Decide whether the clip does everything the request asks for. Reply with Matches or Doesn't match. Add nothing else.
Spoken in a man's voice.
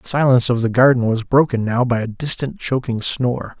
Matches